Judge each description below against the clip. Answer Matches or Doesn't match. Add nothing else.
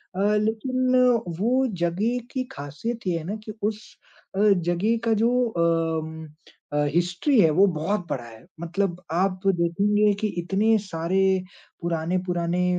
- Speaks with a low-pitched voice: Doesn't match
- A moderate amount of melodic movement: Matches